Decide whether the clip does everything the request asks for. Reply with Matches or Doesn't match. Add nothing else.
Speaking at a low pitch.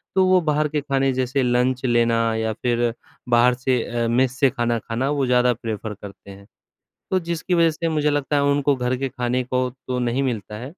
Matches